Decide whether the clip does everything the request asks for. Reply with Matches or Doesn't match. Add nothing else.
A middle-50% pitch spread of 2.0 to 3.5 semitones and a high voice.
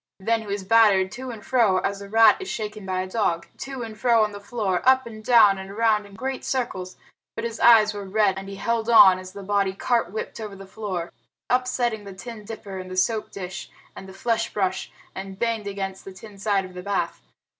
Matches